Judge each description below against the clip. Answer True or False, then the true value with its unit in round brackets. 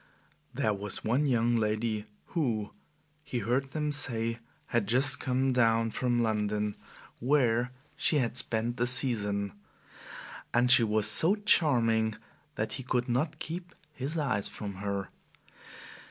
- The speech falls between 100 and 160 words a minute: True (135 wpm)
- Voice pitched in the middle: False (120 Hz)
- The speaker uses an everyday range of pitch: True (3.5 semitones)